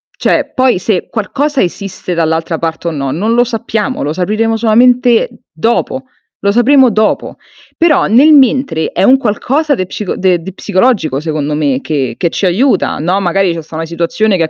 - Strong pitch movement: Yes, wide, 6.5 semitones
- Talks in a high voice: Yes, high, 195 Hz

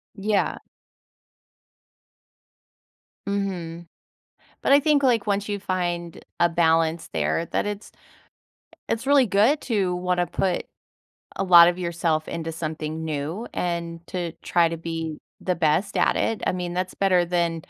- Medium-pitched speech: Yes, medium, 175 Hz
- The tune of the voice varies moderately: Yes, average, 3.1 semitones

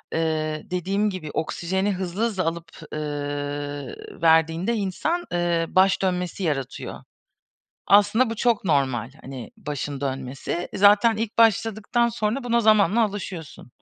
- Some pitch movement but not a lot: No, wide, 5.7 semitones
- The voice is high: No, medium, 180 Hz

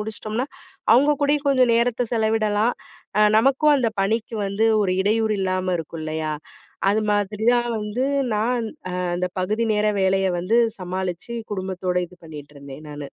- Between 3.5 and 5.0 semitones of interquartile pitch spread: Yes, average, 4.2 semitones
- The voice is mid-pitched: No, high, 210 Hz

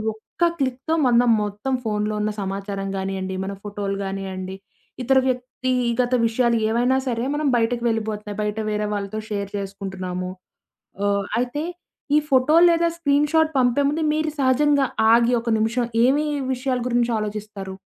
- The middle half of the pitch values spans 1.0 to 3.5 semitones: No, average, 4.2 semitones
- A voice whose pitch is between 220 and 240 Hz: Yes, high, 230 Hz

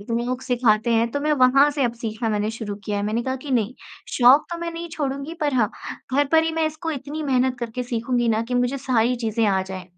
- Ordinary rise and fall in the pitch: Yes, average, 3.9 semitones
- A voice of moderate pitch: No, very high, 250 Hz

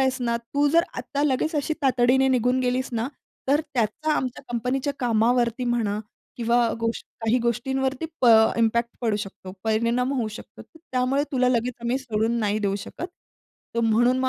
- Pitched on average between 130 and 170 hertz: No, high, 245 Hz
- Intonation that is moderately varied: No, narrow, 2.2 semitones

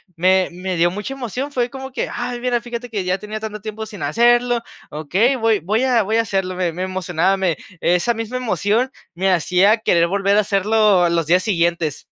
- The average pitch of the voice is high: Yes, high, 205 Hz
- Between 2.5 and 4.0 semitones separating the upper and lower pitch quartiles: No, average, 4.4 semitones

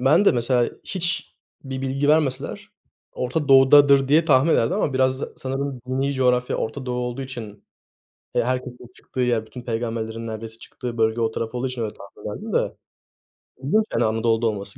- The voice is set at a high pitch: No, low, 125 Hz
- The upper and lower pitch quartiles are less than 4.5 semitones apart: Yes, average, 2.9 semitones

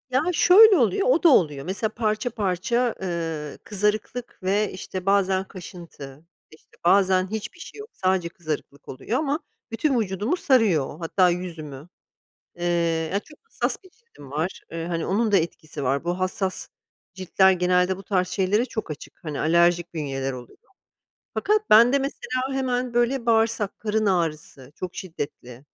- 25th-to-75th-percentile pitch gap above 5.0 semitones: Yes, wide, 5.6 semitones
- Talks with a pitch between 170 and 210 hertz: Yes, high, 190 Hz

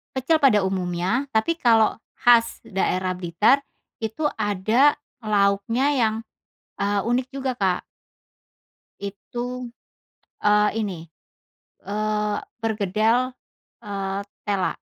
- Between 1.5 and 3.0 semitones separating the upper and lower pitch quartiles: No, average, 3.5 semitones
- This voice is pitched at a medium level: No, high, 215 Hz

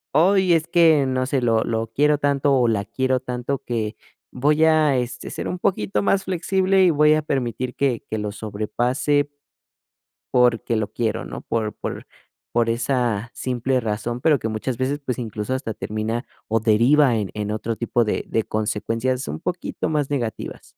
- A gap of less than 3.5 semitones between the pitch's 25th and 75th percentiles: No, average, 4.3 semitones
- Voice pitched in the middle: No, low, 125 Hz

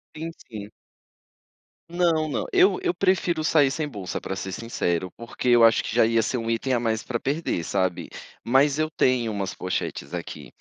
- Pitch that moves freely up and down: Yes, wide, 7.1 semitones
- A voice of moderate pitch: No, low, 120 Hz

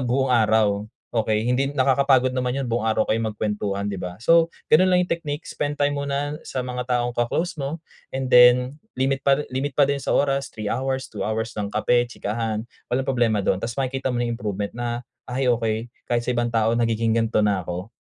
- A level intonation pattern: No, average, 3.5 semitones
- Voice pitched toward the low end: Yes, low, 120 Hz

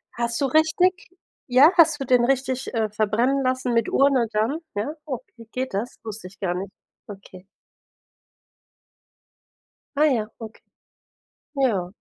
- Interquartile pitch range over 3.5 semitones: Yes, average, 4.2 semitones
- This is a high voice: Yes, high, 245 Hz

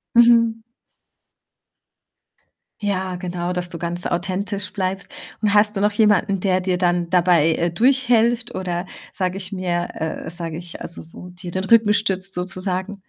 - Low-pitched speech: No, medium, 185 Hz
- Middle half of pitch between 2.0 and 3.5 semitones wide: Yes, average, 2.7 semitones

